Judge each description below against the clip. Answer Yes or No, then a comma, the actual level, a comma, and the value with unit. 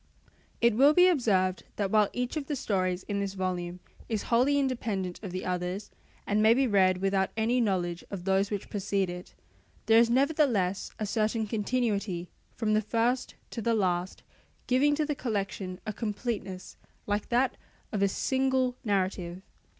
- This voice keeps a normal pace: Yes, average, 165 wpm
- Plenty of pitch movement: No, average, 4.3 semitones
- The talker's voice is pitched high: Yes, high, 210 Hz